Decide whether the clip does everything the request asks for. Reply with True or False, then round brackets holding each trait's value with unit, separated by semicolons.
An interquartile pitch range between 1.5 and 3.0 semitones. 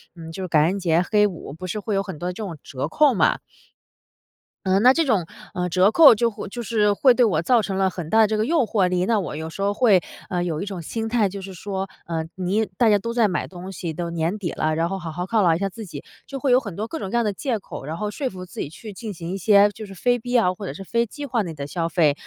False (4.0 semitones)